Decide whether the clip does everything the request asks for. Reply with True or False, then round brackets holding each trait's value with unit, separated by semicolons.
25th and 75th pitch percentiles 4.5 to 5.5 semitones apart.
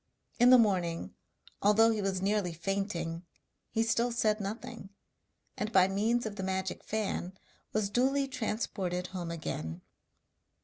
False (3.4 semitones)